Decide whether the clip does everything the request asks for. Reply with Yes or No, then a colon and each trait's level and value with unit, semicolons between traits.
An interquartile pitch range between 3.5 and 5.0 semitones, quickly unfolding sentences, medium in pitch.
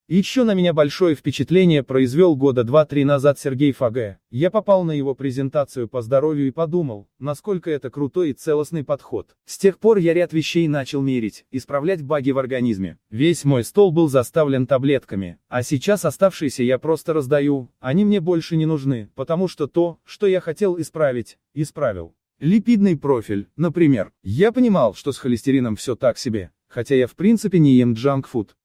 Yes: average, 4.6 semitones; fast, 170 wpm; medium, 145 Hz